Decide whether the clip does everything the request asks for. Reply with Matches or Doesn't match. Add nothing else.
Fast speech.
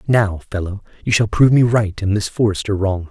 Matches